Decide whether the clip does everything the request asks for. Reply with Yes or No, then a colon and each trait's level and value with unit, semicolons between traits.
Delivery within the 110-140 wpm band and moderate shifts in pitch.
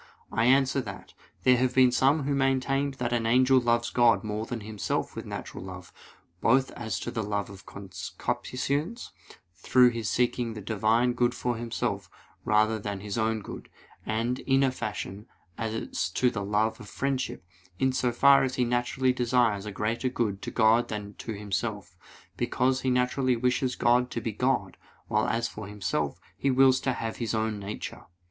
No: average, 180 wpm; average, 3.2 semitones